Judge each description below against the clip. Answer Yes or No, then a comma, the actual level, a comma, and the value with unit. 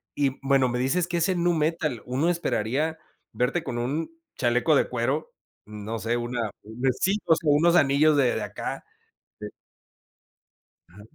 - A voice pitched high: No, low, 135 Hz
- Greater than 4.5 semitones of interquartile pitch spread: Yes, average, 5.2 semitones